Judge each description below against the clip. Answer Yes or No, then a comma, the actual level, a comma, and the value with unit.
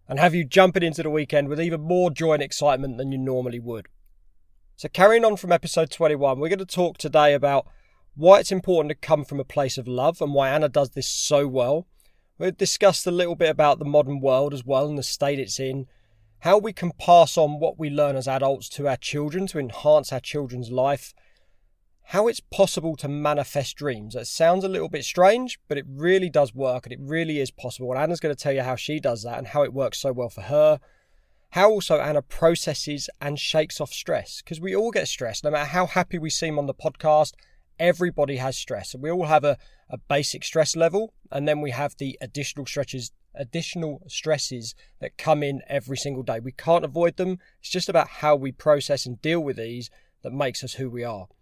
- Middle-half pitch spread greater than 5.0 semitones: No, average, 3.8 semitones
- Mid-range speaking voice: Yes, medium, 145 Hz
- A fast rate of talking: Yes, fast, 220 wpm